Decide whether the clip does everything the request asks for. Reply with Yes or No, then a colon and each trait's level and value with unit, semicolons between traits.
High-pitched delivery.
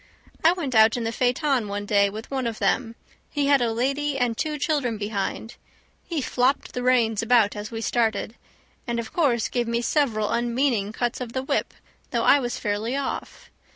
Yes: high, 240 Hz